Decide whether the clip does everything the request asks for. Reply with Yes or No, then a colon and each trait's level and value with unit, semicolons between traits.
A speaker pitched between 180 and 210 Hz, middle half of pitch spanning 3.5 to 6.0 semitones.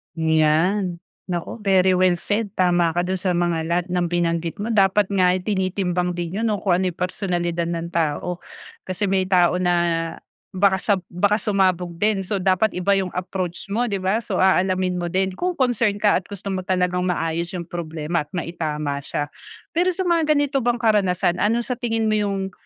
No: medium, 185 Hz; average, 2.7 semitones